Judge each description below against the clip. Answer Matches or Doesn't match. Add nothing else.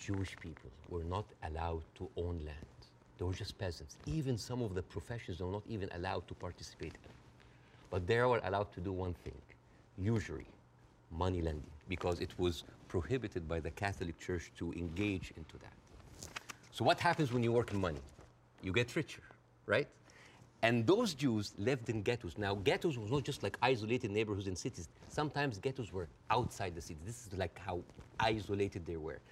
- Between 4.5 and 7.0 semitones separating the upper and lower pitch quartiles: Matches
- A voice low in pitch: Matches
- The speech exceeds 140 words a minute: Matches